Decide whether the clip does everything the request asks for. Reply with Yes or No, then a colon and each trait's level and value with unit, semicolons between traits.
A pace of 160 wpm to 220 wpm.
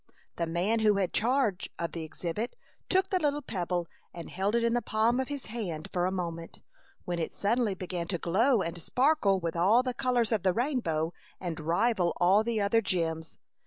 Yes: average, 200 wpm